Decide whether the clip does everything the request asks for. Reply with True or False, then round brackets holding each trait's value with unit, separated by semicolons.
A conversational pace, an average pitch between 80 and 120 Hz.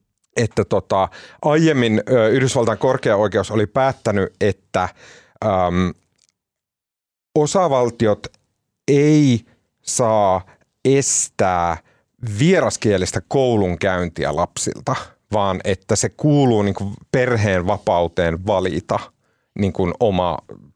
False (80 wpm; 110 Hz)